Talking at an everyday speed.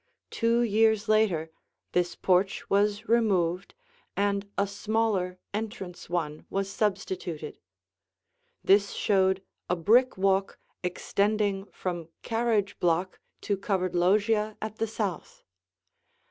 No: slow, 105 wpm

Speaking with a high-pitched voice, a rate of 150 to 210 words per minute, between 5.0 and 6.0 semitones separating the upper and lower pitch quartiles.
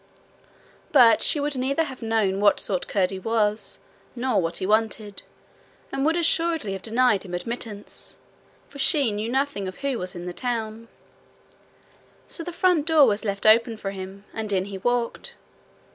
Yes: high, 225 Hz; average, 165 wpm; average, 5.3 semitones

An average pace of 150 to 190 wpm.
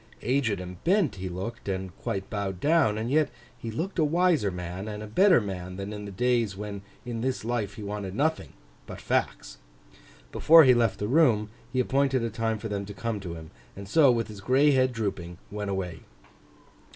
No: average, 200 wpm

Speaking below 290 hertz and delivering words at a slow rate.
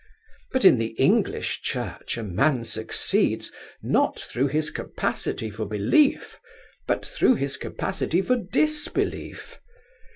Yes: medium, 140 Hz; slow, 120 wpm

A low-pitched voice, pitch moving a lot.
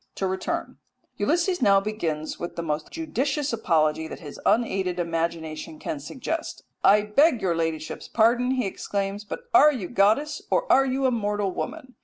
No: high, 205 Hz; wide, 7.5 semitones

